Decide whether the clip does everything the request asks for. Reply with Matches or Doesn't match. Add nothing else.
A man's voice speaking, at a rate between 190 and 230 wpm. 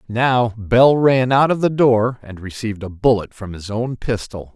Matches